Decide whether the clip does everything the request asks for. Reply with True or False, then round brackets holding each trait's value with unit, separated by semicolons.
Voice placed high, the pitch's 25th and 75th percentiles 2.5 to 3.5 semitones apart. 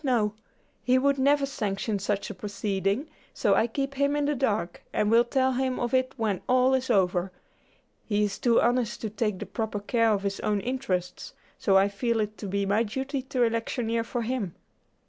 False (230 Hz; 4.2 semitones)